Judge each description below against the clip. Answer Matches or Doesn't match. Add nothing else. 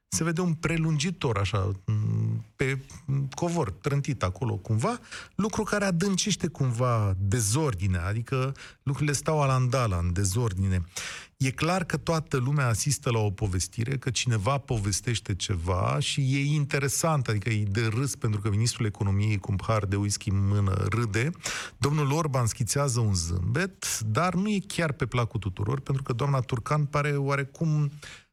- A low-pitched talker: Matches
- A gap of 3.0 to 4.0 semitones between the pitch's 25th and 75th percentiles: Doesn't match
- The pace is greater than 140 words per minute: Matches